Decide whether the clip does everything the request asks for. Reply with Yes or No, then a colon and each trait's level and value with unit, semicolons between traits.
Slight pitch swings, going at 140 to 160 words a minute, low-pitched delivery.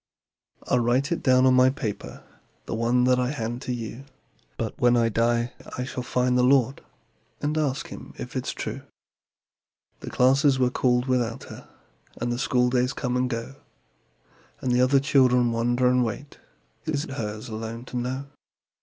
No: narrow, 1.5 semitones; average, 170 wpm; low, 125 Hz